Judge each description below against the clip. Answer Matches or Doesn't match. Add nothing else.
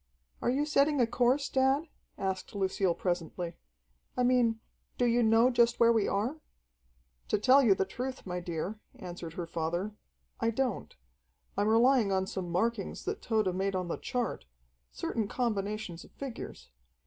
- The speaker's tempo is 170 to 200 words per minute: Doesn't match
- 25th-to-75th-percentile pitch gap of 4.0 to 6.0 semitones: Matches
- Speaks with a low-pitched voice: Doesn't match